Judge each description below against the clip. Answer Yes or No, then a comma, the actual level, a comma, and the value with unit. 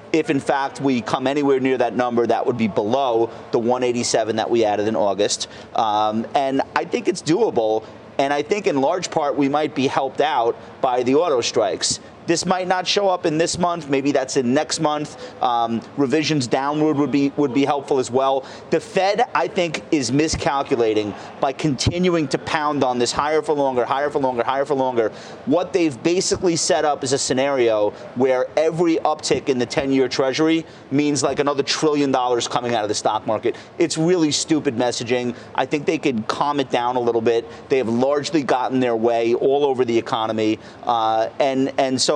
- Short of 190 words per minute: No, average, 200 wpm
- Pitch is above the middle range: No, low, 135 Hz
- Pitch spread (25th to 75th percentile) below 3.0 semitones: No, average, 4.1 semitones